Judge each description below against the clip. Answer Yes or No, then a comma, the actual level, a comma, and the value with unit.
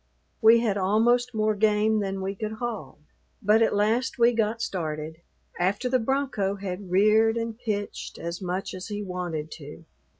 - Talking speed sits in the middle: Yes, average, 165 wpm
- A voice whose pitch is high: Yes, high, 210 Hz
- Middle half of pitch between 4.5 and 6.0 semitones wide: No, average, 3.2 semitones